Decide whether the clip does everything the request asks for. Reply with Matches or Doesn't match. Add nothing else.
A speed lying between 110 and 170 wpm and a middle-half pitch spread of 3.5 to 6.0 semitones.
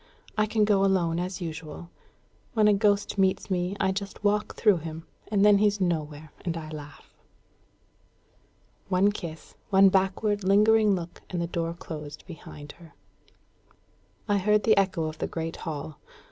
Matches